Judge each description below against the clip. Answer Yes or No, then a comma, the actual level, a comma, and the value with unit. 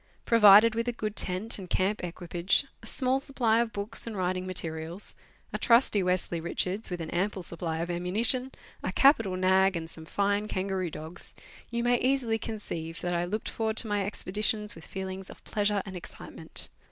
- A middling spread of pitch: Yes, average, 3.8 semitones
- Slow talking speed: No, average, 180 wpm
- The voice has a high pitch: Yes, high, 195 Hz